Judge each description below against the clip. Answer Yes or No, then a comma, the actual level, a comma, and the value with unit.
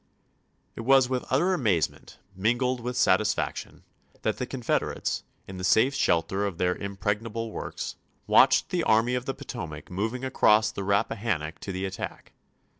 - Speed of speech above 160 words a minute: No, average, 155 wpm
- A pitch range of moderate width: Yes, average, 4.7 semitones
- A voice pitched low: Yes, low, 110 Hz